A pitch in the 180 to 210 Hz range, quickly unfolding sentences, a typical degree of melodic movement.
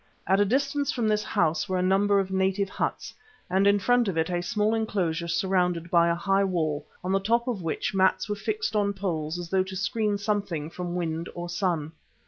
Yes: high, 190 Hz; fast, 215 wpm; average, 3.1 semitones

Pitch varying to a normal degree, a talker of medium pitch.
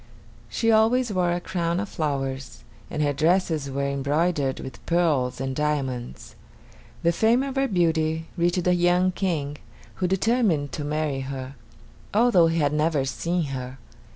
Yes: average, 4.4 semitones; medium, 160 Hz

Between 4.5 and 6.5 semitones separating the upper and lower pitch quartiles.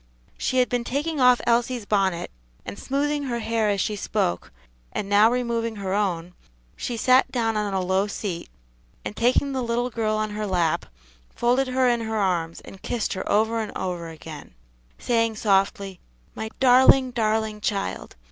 No: average, 3.8 semitones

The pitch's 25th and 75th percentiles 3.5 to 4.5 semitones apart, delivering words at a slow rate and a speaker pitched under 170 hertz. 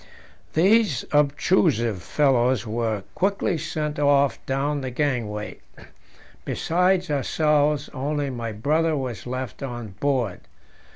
Yes: average, 4.0 semitones; slow, 105 wpm; medium, 140 Hz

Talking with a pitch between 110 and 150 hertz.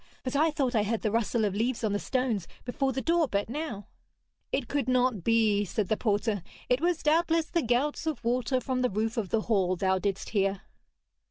No: high, 235 Hz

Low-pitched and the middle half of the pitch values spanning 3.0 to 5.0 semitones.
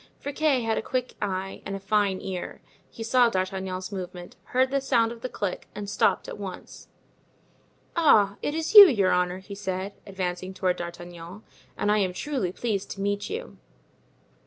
No: high, 200 Hz; average, 4.2 semitones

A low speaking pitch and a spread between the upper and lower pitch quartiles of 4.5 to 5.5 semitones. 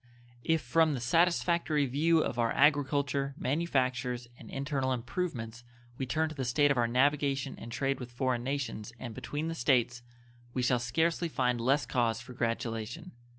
No: low, 130 Hz; average, 3.4 semitones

